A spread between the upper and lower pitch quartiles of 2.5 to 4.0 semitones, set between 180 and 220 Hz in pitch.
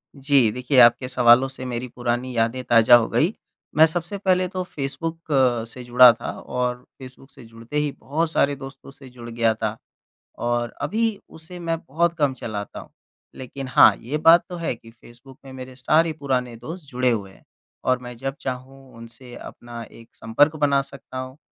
No: average, 3.5 semitones; low, 130 Hz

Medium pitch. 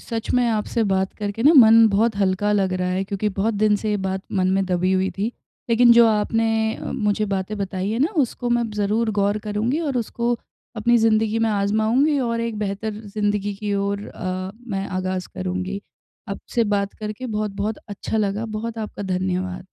No: high, 210 Hz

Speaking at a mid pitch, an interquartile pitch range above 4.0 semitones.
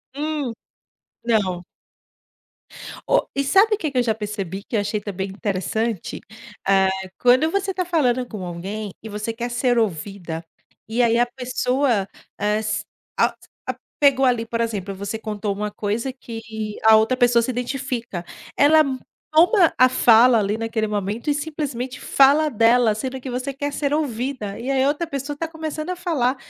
No: high, 240 Hz; average, 4.7 semitones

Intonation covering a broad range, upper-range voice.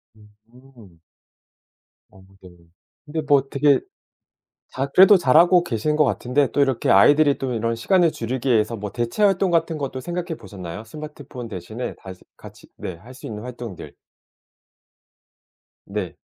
No: wide, 5.9 semitones; low, 125 Hz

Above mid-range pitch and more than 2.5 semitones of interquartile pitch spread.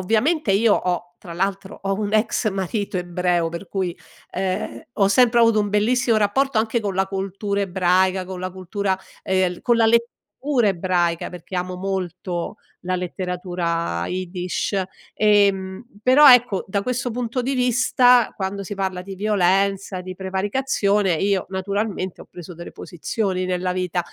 Yes: high, 195 Hz; average, 2.9 semitones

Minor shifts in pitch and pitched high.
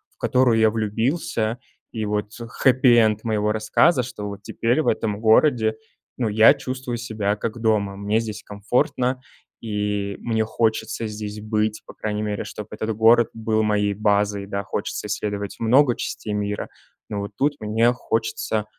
No: narrow, 1.8 semitones; low, 110 Hz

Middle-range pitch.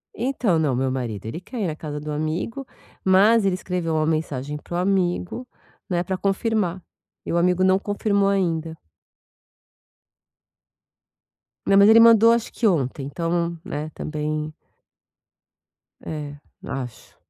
Yes: medium, 175 Hz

